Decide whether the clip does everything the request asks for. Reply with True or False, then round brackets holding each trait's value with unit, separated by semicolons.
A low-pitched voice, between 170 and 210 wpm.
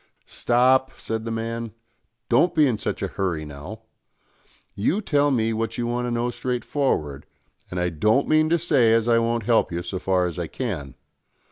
True (115 Hz; 190 wpm)